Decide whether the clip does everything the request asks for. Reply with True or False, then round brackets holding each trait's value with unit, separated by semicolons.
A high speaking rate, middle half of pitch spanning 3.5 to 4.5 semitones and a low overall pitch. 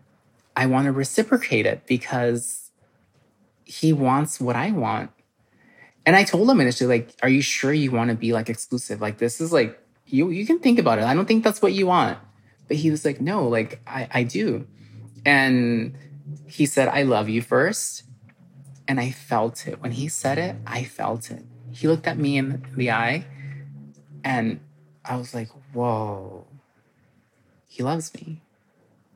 False (175 wpm; 4.1 semitones; 130 Hz)